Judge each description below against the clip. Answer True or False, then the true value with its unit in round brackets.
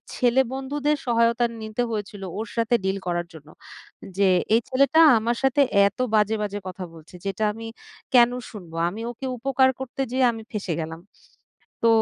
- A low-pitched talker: False (225 Hz)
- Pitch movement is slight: False (4.3 semitones)